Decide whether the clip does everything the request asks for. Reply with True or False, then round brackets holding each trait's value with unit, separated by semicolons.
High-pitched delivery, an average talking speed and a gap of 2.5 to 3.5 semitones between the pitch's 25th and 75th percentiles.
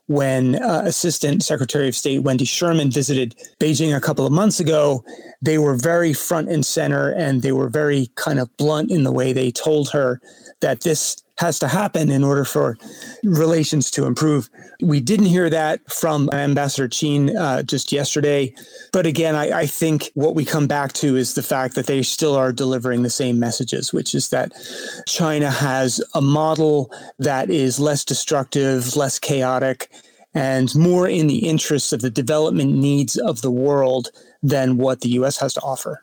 False (145 Hz; 180 wpm; 2.9 semitones)